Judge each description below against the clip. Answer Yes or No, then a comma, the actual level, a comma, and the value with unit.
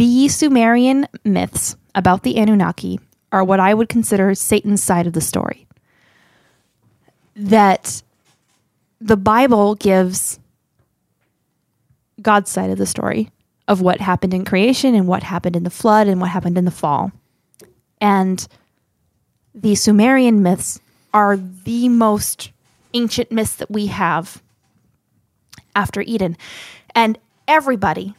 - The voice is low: No, high, 200 Hz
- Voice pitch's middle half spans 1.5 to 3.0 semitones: No, average, 3.6 semitones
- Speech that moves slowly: Yes, slow, 125 wpm